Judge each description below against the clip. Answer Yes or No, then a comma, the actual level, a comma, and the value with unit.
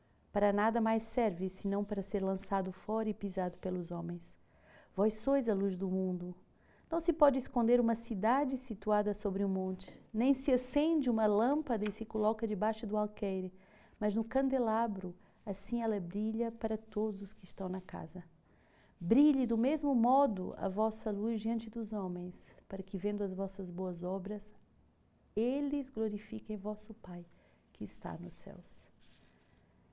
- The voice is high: Yes, high, 210 Hz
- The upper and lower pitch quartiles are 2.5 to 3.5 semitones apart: Yes, average, 3.2 semitones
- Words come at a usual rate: Yes, average, 155 wpm